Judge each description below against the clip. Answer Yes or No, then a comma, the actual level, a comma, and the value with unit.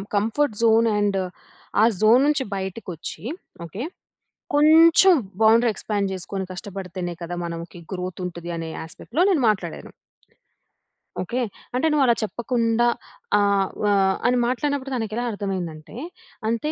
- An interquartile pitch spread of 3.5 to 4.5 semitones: No, average, 5.1 semitones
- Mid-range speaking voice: No, high, 215 Hz